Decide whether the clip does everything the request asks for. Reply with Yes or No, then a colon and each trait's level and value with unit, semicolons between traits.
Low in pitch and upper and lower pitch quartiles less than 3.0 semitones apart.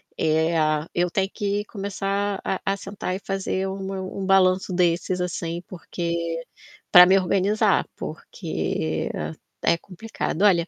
No: medium, 185 Hz; narrow, 2.5 semitones